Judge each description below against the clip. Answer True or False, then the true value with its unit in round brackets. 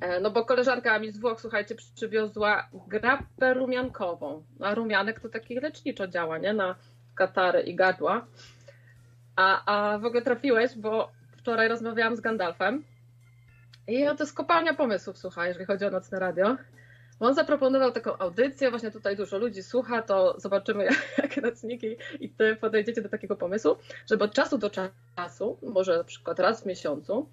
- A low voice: False (210 Hz)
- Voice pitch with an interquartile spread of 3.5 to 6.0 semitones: True (4.7 semitones)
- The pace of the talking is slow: False (160 wpm)